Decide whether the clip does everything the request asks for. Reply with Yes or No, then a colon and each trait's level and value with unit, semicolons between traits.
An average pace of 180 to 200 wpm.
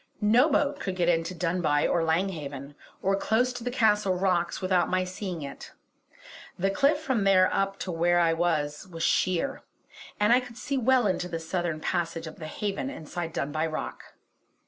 Yes: average, 185 wpm